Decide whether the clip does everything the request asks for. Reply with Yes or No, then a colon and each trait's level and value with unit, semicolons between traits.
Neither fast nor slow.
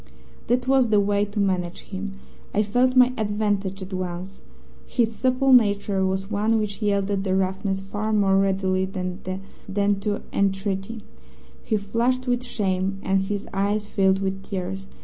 Yes: average, 150 wpm